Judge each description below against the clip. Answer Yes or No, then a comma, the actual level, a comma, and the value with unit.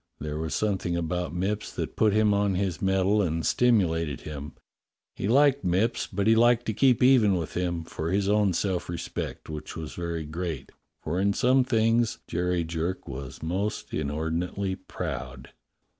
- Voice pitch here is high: No, very low, 90 Hz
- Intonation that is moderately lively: Yes, average, 4.4 semitones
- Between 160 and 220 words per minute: Yes, average, 165 wpm